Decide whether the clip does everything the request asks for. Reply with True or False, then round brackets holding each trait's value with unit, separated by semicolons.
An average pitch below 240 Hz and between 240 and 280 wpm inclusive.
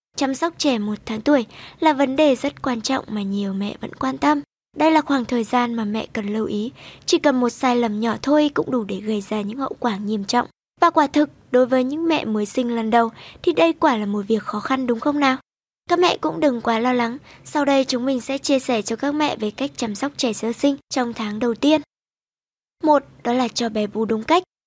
False (255 Hz; 250 wpm)